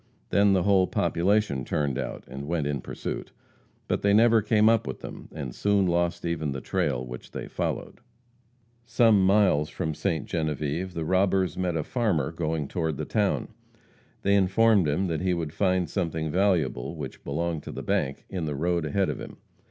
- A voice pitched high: No, very low, 85 Hz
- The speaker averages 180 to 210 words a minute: Yes, average, 185 wpm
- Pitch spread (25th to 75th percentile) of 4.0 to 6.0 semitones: Yes, average, 4.5 semitones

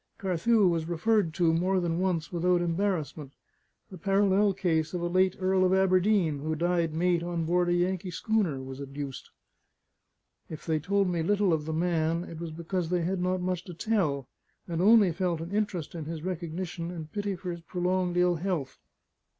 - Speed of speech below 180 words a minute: No, average, 185 wpm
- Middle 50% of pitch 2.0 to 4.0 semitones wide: Yes, narrow, 2.4 semitones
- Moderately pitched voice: Yes, medium, 175 Hz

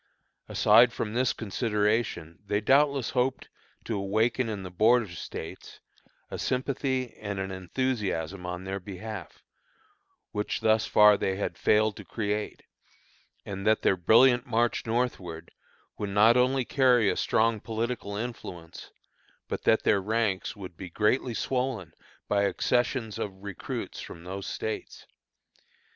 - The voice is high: No, low, 110 Hz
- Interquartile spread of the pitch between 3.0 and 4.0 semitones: Yes, average, 3.7 semitones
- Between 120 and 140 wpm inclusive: Yes, slow, 135 wpm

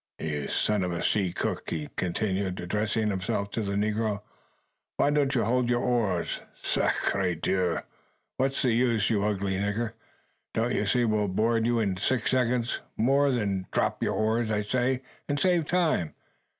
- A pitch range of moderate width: Yes, average, 4.0 semitones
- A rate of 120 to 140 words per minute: No, average, 165 wpm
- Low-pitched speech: Yes, low, 110 Hz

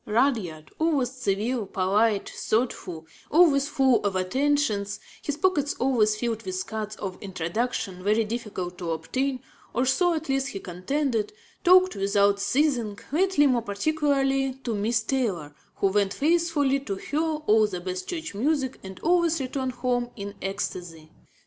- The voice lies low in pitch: No, high, 235 Hz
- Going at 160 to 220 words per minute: No, average, 145 wpm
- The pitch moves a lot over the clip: Yes, wide, 5.8 semitones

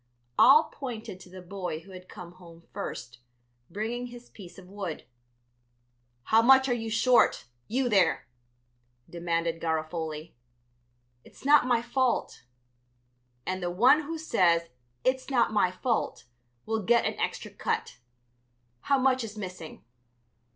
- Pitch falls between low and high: No, high, 205 Hz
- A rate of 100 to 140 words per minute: Yes, slow, 135 wpm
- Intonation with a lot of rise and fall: Yes, wide, 6.0 semitones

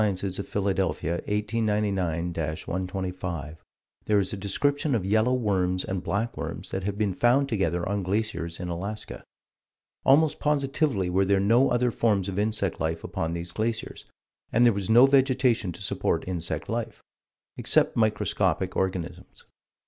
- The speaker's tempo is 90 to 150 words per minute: Yes, average, 145 wpm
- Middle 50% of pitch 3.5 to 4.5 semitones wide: Yes, average, 3.9 semitones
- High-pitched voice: No, low, 100 Hz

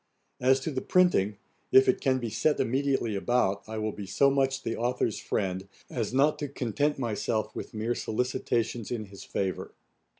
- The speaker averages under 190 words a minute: Yes, average, 175 wpm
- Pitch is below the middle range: Yes, low, 120 Hz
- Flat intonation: No, average, 3.9 semitones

